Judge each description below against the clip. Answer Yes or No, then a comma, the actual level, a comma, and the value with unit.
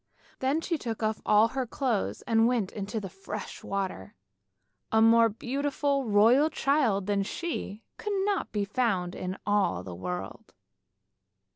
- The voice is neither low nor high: No, high, 220 Hz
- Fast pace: No, average, 145 wpm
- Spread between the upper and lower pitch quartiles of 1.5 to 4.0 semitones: No, average, 5.1 semitones